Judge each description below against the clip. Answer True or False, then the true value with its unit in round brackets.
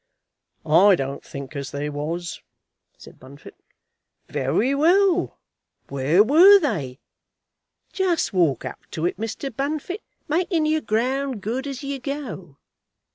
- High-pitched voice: True (225 Hz)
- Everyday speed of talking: False (125 wpm)